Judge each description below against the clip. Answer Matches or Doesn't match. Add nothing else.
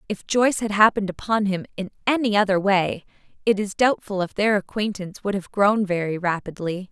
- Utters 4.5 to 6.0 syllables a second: Matches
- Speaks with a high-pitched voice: Matches